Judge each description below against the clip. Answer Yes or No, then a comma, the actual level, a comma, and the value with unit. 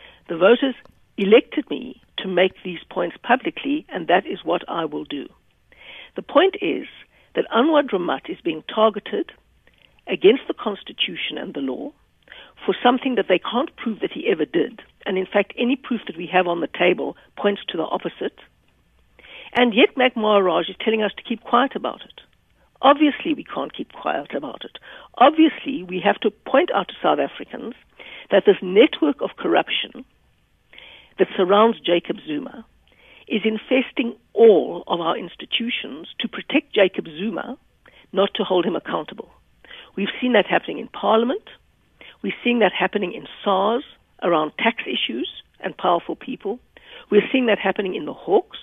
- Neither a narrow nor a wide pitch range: No, wide, 6.0 semitones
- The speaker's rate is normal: Yes, average, 165 wpm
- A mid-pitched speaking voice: No, high, 230 Hz